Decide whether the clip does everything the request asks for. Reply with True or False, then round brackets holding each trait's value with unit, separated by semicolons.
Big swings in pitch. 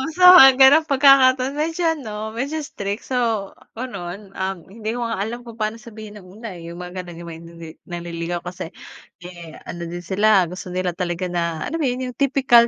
True (6.2 semitones)